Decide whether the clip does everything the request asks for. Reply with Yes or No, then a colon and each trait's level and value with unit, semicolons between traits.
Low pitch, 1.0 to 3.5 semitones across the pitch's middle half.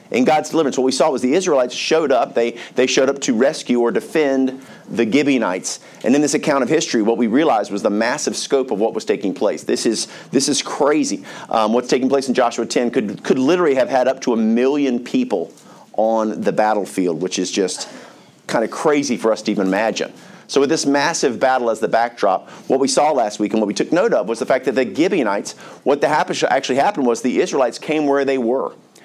Yes: low, 125 Hz; average, 2.8 semitones